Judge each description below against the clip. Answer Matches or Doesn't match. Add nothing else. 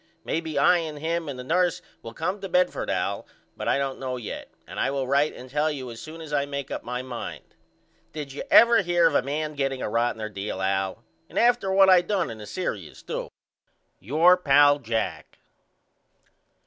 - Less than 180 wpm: Doesn't match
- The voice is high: Doesn't match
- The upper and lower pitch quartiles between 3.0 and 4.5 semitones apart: Doesn't match